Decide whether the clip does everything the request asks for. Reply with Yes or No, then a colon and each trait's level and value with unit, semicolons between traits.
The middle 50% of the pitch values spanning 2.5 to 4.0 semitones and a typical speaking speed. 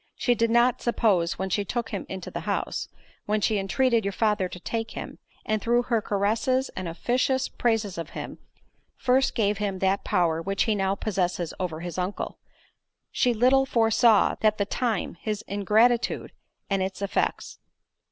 Yes: average, 3.6 semitones; average, 170 wpm